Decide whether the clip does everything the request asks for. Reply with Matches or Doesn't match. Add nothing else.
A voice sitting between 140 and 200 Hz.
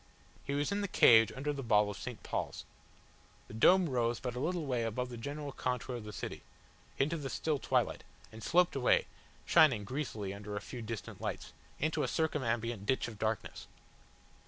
Doesn't match